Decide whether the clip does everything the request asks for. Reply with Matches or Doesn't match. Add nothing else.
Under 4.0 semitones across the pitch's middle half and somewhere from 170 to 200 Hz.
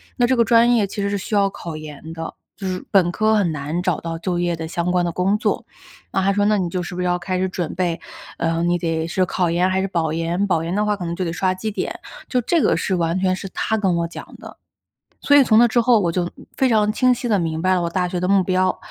Matches